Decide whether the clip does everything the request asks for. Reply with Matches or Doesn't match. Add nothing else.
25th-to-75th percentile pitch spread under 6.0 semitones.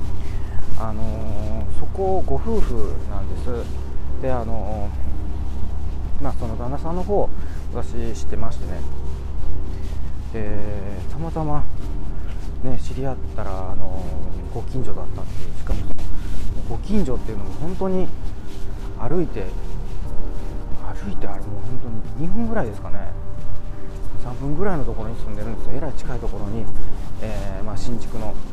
Matches